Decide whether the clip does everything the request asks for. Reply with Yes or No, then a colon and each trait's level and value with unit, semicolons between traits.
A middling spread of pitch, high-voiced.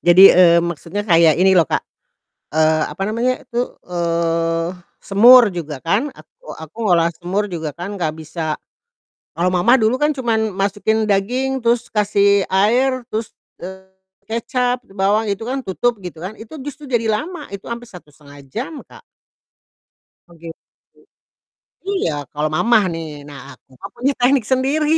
No: wide, 6.0 semitones; high, 200 Hz